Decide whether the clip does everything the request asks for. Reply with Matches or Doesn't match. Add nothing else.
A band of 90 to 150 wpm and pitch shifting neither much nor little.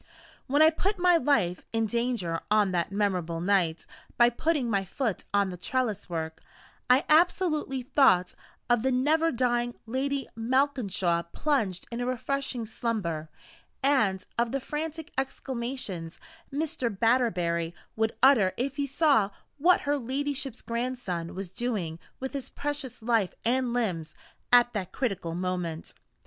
Doesn't match